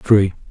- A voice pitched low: Yes, low, 100 Hz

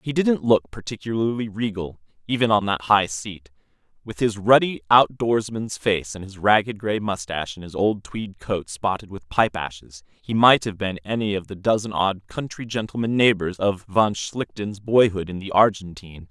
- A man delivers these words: Yes, male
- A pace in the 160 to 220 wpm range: Yes, average, 175 wpm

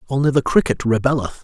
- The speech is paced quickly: No, average, 165 wpm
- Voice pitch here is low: Yes, low, 130 Hz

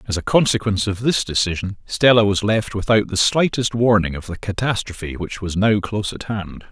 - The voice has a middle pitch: No, low, 105 Hz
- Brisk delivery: No, average, 195 wpm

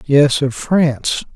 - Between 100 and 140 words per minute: Yes, slow, 135 wpm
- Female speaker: No, male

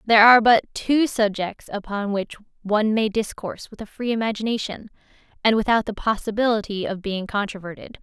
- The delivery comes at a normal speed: Yes, average, 155 wpm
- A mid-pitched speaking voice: No, high, 215 Hz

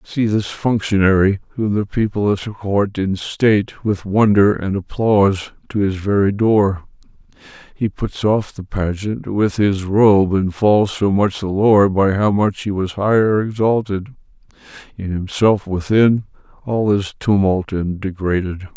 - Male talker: Yes, male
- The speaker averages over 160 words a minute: No, average, 145 wpm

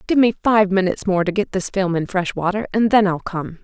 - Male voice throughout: No, female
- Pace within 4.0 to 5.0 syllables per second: No, 5.7 syllables/s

